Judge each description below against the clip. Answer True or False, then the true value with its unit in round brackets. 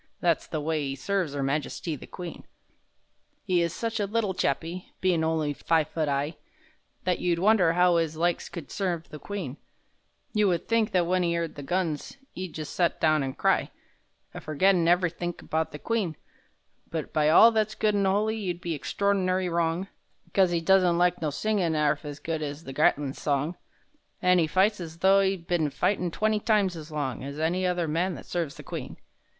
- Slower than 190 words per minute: False (195 wpm)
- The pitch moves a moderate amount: True (3.3 semitones)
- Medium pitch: True (170 Hz)